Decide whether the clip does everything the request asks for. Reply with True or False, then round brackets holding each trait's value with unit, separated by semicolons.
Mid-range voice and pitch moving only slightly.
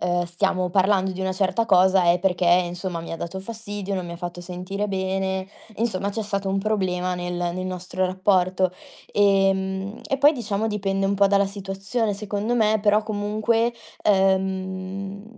False (195 Hz; 1.8 semitones)